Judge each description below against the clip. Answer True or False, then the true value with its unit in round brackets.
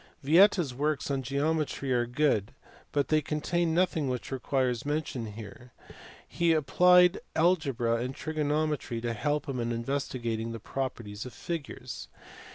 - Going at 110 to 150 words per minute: True (140 wpm)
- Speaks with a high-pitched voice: False (140 Hz)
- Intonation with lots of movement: False (4.4 semitones)